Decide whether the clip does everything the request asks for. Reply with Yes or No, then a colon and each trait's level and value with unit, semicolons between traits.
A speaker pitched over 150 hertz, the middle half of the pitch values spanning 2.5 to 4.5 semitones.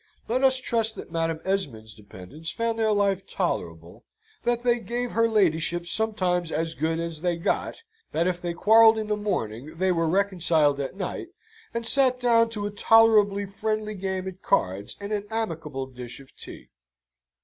No: high, 190 Hz; wide, 5.4 semitones